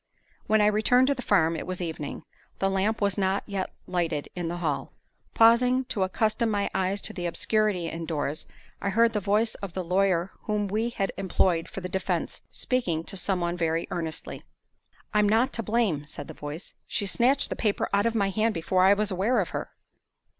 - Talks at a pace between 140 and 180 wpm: No, average, 200 wpm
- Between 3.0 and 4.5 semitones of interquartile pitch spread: Yes, average, 3.8 semitones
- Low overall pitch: No, high, 195 Hz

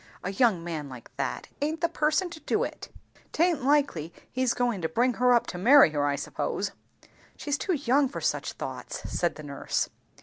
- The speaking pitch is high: Yes, high, 245 Hz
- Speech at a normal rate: Yes, average, 195 wpm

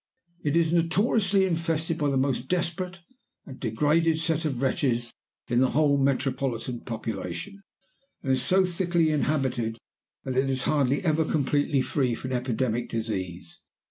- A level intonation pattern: No, average, 4.7 semitones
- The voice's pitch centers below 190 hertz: Yes, medium, 140 Hz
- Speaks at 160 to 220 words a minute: No, average, 145 wpm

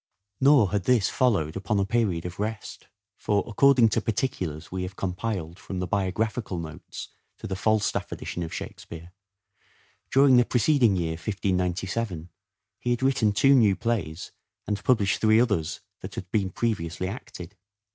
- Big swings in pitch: No, average, 4.3 semitones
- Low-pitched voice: Yes, low, 100 Hz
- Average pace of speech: Yes, average, 155 wpm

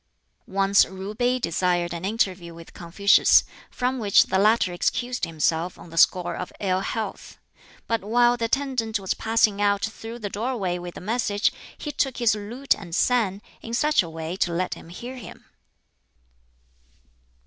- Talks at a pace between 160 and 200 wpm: Yes, average, 170 wpm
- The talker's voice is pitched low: No, high, 205 Hz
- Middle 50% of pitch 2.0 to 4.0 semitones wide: No, average, 4.6 semitones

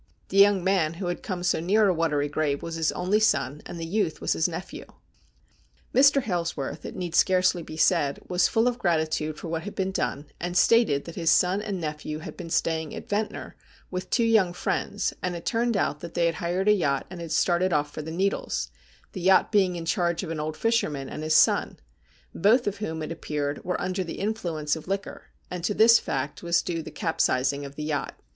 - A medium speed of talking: No, fast, 220 wpm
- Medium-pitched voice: Yes, medium, 175 Hz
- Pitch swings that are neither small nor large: Yes, average, 3.7 semitones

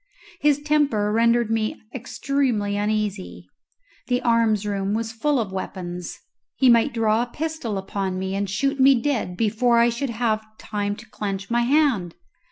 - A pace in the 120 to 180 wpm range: Yes, average, 160 wpm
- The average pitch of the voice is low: No, high, 225 Hz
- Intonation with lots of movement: No, average, 3.4 semitones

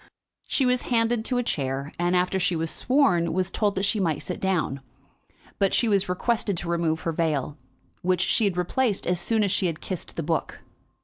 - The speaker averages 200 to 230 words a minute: Yes, fast, 205 wpm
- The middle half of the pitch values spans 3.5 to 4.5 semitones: Yes, average, 4.1 semitones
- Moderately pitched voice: Yes, medium, 180 Hz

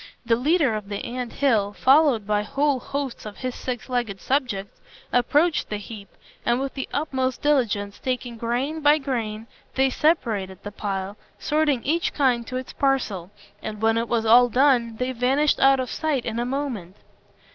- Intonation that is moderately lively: Yes, average, 4.1 semitones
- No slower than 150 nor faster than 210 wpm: Yes, average, 175 wpm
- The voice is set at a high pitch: Yes, high, 245 Hz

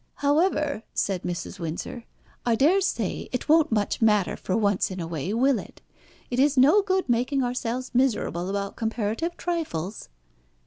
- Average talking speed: Yes, average, 150 wpm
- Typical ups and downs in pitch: No, wide, 6.3 semitones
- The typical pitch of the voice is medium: No, high, 240 Hz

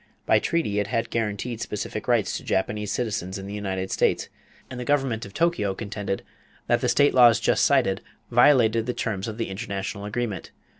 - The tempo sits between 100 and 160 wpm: No, average, 185 wpm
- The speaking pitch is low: Yes, low, 110 Hz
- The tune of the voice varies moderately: Yes, average, 3.4 semitones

